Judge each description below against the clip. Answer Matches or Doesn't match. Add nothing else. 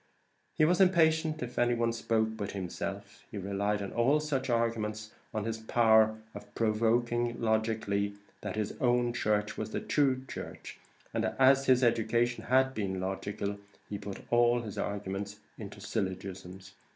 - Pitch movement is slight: Doesn't match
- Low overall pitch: Matches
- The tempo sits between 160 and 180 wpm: Doesn't match